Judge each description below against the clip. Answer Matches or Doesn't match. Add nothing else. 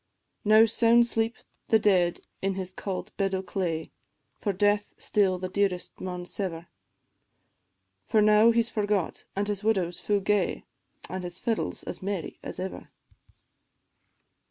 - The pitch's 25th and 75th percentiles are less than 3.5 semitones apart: Matches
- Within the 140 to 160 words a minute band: Matches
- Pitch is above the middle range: Matches